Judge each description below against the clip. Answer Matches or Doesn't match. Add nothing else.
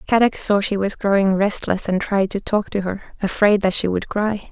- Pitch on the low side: Doesn't match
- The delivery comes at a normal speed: Doesn't match